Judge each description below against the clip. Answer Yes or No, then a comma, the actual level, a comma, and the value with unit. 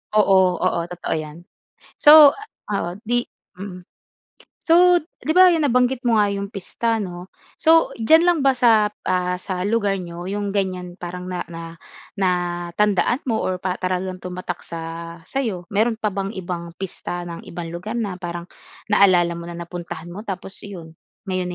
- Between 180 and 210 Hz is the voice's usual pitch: Yes, high, 190 Hz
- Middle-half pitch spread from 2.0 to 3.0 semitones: No, average, 4.0 semitones